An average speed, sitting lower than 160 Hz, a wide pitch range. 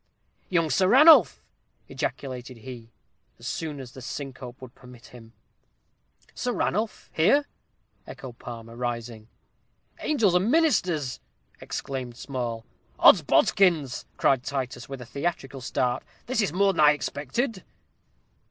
No: slow, 120 wpm; low, 135 Hz; wide, 6.7 semitones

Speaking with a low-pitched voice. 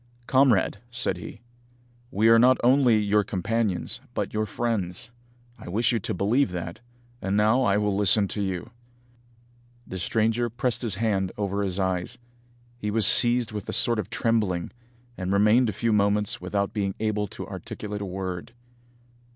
Yes: low, 105 Hz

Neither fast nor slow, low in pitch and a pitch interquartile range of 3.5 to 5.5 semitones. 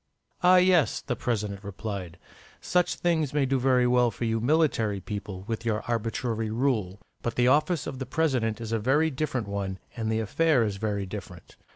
Yes: average, 185 wpm; low, 115 Hz; average, 4.4 semitones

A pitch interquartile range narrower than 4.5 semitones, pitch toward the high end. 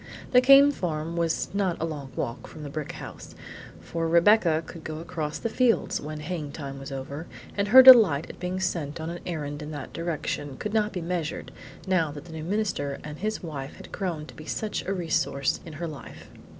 No: average, 3.9 semitones; medium, 165 Hz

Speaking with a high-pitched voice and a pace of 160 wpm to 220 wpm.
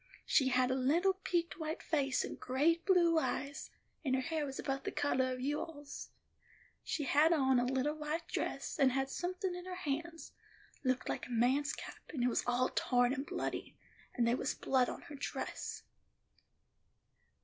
Yes: very high, 280 Hz; average, 180 wpm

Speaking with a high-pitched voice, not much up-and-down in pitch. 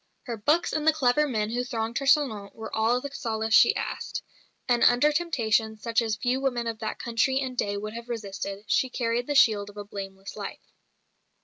No: high, 230 Hz; average, 3.3 semitones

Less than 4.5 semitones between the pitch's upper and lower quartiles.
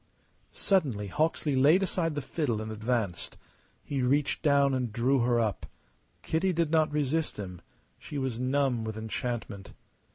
No: average, 5.1 semitones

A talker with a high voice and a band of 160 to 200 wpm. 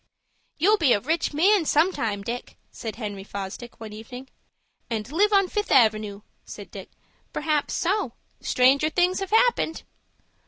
No: very high, 275 Hz; average, 150 wpm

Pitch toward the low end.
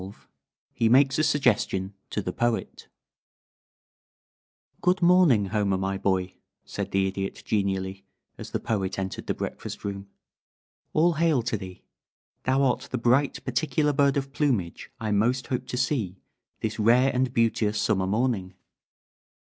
Yes: low, 115 Hz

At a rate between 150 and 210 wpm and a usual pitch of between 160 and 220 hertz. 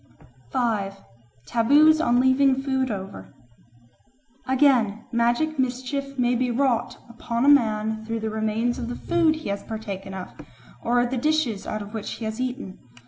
No: average, 155 wpm; high, 240 Hz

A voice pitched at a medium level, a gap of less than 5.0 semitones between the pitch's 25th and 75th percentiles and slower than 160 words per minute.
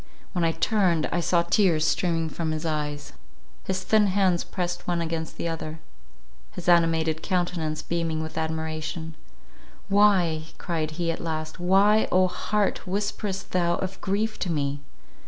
Yes: medium, 170 Hz; average, 2.8 semitones; average, 150 wpm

